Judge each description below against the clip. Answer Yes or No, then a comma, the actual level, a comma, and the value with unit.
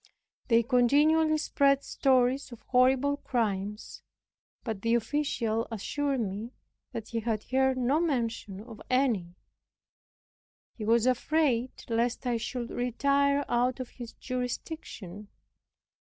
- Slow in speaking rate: Yes, slow, 115 wpm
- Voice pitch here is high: Yes, high, 245 Hz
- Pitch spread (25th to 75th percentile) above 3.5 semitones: No, average, 3.2 semitones